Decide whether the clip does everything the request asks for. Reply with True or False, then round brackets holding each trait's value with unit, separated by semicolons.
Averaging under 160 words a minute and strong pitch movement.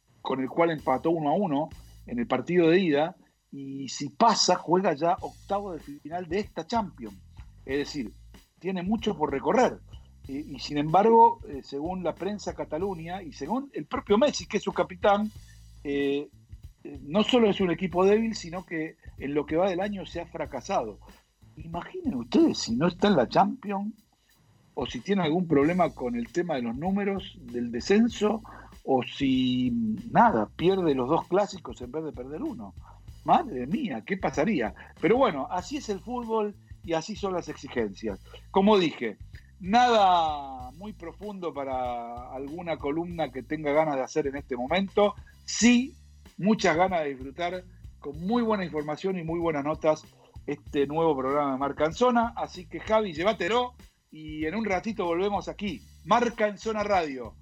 False (170 wpm; 6.4 semitones)